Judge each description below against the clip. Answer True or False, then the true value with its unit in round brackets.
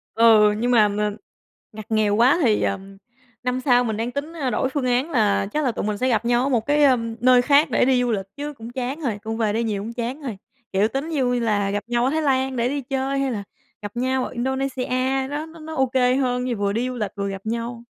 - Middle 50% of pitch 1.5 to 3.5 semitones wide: True (3.2 semitones)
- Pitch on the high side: True (245 Hz)